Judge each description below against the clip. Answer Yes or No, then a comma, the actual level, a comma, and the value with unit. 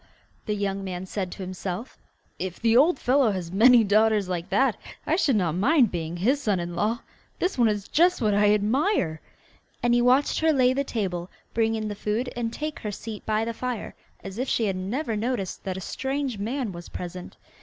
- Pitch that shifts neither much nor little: Yes, average, 4.8 semitones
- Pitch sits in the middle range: No, high, 215 Hz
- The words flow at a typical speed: No, fast, 210 wpm